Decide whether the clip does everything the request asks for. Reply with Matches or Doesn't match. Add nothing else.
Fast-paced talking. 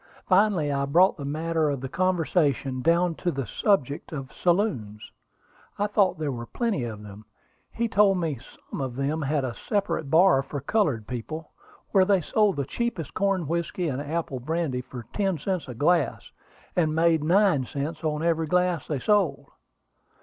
Doesn't match